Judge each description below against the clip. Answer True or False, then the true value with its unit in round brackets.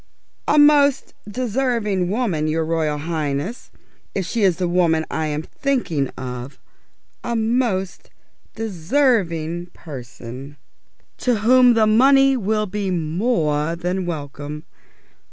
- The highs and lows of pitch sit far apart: True (7.1 semitones)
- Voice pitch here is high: False (180 Hz)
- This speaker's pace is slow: True (110 wpm)